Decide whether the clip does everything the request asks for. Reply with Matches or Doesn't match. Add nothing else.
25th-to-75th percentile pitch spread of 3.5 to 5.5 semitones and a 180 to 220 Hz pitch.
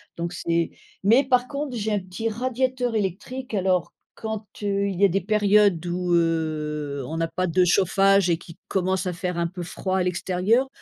Matches